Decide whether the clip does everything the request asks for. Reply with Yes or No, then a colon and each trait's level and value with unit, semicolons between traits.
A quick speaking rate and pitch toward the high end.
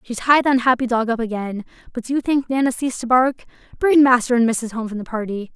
Yes: fast, 250 wpm; high, 245 Hz